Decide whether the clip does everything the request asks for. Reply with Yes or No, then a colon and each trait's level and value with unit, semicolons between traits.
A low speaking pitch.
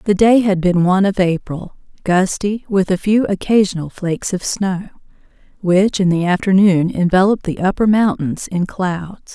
No: high, 190 Hz